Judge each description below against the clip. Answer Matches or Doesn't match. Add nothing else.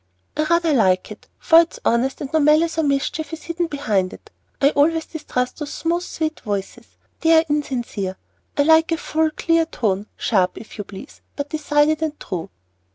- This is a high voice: Matches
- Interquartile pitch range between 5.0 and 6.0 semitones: Matches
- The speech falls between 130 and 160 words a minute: Doesn't match